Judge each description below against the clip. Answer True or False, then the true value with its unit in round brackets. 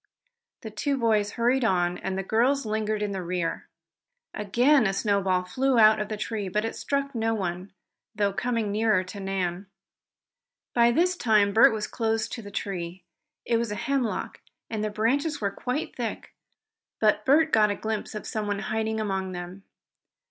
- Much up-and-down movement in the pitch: False (2.9 semitones)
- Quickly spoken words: False (170 wpm)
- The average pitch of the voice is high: True (215 Hz)